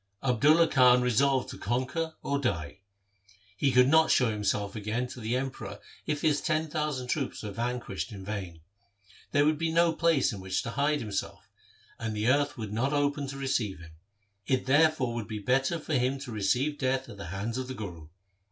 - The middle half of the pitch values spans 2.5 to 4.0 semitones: No, average, 4.9 semitones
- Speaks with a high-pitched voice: No, low, 130 Hz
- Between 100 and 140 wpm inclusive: No, average, 200 wpm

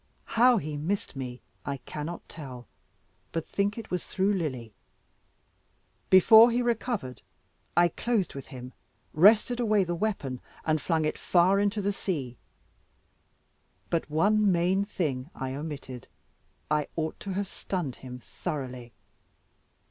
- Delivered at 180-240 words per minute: No, slow, 135 wpm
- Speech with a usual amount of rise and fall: No, wide, 6.8 semitones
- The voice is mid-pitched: Yes, medium, 170 Hz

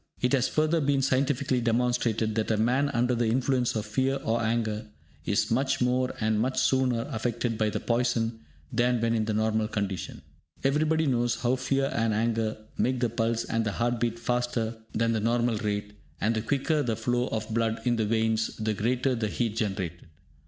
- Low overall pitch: Yes, low, 115 Hz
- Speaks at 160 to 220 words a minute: Yes, average, 190 wpm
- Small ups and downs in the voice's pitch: Yes, narrow, 2.2 semitones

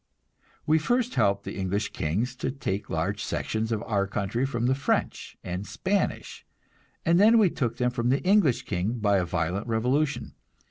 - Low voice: Yes, low, 120 Hz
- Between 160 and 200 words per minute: Yes, average, 175 wpm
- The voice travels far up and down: Yes, wide, 6.1 semitones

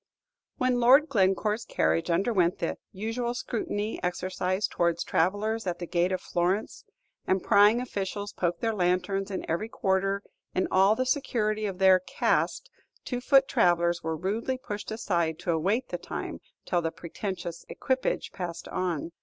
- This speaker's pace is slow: No, average, 155 wpm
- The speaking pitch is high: Yes, high, 195 Hz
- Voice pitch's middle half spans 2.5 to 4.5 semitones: Yes, average, 3.9 semitones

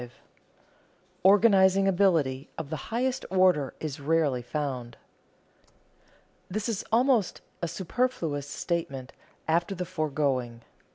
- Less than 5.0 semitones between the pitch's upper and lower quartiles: No, wide, 5.5 semitones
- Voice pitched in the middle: Yes, medium, 165 Hz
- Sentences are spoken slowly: Yes, slow, 100 wpm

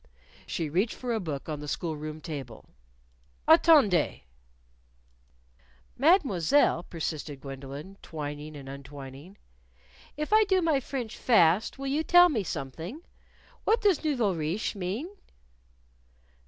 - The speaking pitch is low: No, medium, 180 Hz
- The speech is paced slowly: Yes, slow, 120 wpm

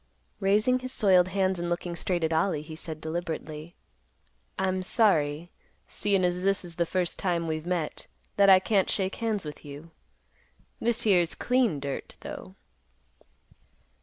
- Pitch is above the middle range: No, medium, 180 Hz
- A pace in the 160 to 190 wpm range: No, average, 150 wpm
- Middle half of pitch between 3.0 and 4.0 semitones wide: Yes, average, 3.4 semitones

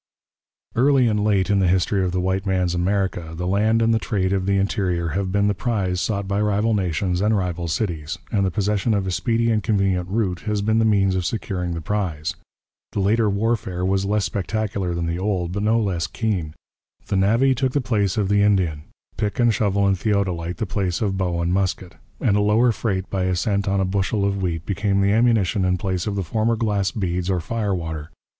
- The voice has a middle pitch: No, low, 100 Hz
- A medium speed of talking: No, fast, 220 wpm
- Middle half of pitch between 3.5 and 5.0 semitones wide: No, narrow, 2.6 semitones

